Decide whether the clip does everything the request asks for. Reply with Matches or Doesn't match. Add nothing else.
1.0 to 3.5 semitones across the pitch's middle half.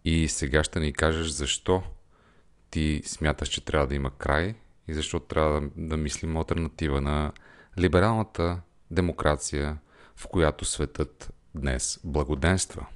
Matches